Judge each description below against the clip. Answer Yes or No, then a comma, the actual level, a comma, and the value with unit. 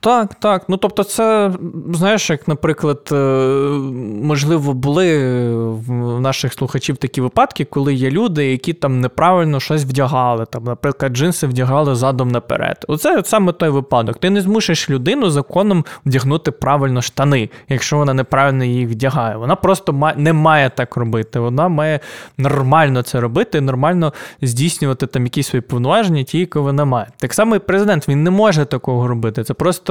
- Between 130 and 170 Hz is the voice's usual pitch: Yes, medium, 140 Hz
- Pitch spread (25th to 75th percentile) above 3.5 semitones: Yes, average, 4.2 semitones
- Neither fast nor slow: No, fast, 160 wpm